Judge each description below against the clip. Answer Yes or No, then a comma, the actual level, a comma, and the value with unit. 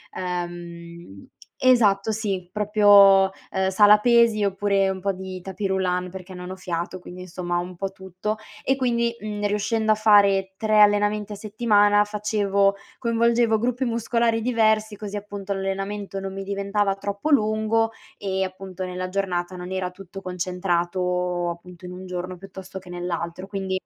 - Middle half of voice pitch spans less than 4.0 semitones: Yes, narrow, 2.5 semitones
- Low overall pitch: No, high, 195 Hz